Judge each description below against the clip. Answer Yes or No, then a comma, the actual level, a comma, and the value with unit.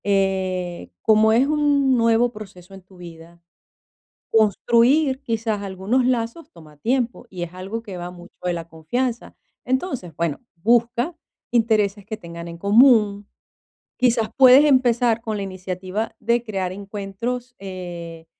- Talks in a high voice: Yes, high, 210 Hz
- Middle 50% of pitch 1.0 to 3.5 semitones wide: No, average, 4.7 semitones